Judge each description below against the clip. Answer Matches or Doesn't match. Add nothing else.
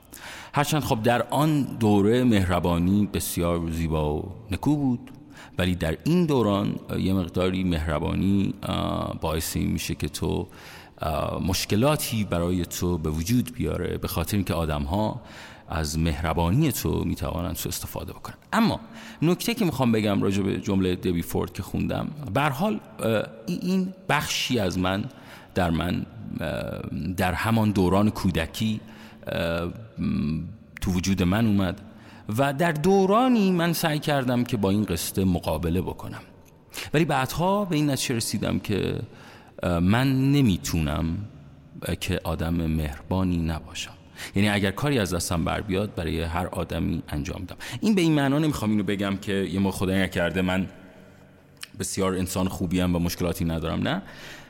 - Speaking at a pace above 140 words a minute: Doesn't match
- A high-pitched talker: Doesn't match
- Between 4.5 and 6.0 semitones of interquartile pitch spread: Matches